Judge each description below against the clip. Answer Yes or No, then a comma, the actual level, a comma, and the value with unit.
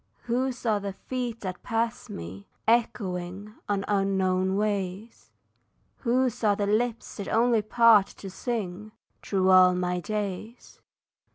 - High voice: Yes, high, 205 Hz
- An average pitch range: Yes, average, 3.6 semitones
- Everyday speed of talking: No, slow, 125 wpm